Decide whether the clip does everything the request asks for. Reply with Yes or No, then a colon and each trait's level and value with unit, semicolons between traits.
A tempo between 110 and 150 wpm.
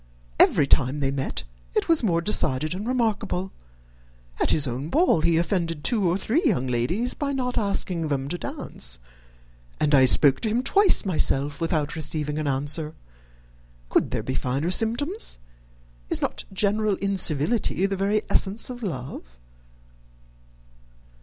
Yes: average, 145 wpm